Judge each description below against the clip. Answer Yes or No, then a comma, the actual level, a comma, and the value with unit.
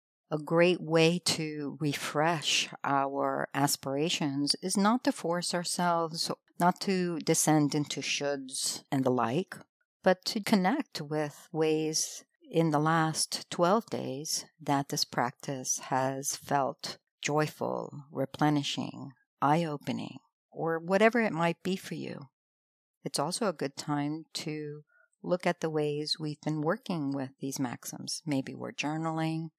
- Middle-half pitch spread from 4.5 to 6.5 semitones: No, average, 3.4 semitones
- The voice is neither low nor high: Yes, medium, 155 Hz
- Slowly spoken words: Yes, slow, 130 wpm